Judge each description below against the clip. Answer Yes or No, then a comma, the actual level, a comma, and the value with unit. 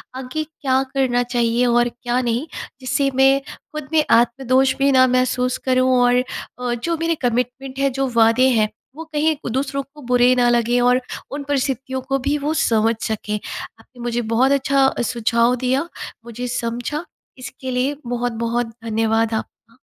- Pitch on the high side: Yes, very high, 250 Hz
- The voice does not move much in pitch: Yes, narrow, 2.2 semitones